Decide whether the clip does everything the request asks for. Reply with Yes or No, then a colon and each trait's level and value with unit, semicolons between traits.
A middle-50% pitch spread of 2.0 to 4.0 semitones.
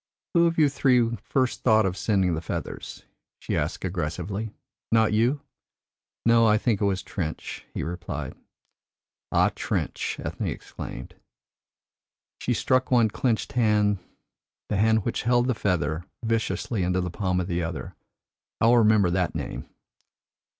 No: average, 4.5 semitones